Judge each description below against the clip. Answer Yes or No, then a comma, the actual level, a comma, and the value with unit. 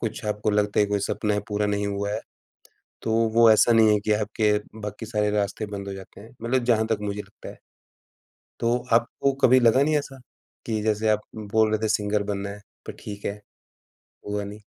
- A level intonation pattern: Yes, narrow, 1.6 semitones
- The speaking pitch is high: No, low, 105 Hz